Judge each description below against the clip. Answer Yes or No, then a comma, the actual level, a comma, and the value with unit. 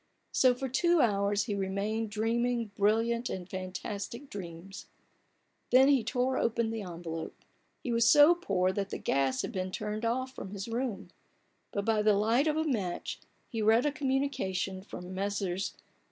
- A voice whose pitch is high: Yes, high, 215 Hz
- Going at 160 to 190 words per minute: Yes, average, 165 wpm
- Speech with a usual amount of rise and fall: Yes, average, 4.3 semitones